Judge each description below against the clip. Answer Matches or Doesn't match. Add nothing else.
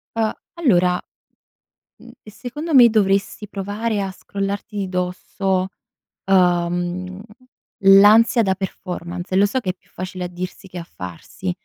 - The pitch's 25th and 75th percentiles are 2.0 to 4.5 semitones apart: Matches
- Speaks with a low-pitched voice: Doesn't match